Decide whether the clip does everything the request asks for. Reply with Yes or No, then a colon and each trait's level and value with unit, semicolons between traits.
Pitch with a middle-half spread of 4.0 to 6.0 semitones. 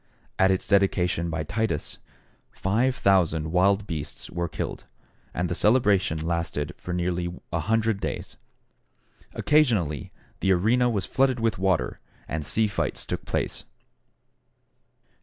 Yes: average, 4.4 semitones